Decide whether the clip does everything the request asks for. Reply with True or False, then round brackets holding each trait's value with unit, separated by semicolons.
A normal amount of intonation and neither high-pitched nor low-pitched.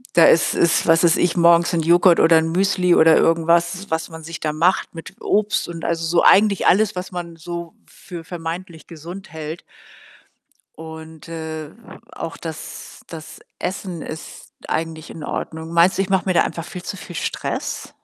False (1.7 semitones; 170 Hz)